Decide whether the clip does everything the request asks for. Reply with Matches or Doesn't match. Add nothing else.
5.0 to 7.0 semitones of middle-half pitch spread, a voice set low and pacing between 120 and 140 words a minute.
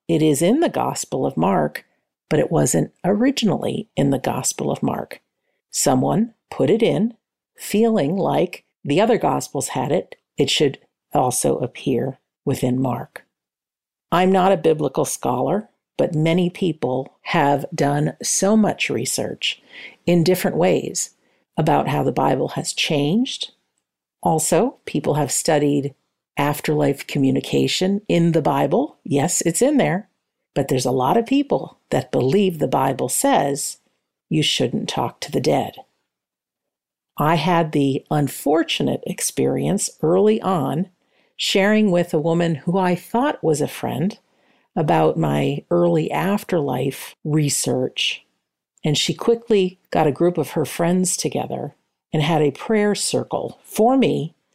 Doesn't match